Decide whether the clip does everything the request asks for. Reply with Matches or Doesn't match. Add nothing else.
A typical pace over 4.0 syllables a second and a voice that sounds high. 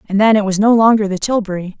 Matches